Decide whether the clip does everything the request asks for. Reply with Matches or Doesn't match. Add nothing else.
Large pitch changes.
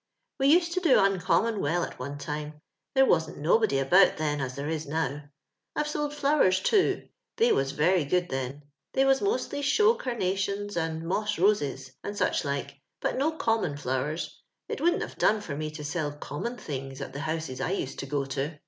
Matches